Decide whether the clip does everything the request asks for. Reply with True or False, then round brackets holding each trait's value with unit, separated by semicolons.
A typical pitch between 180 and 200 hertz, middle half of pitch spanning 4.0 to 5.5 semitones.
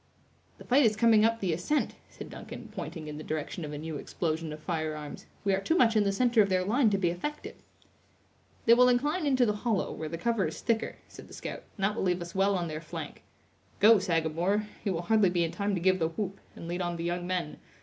True (190 Hz; 4.8 semitones)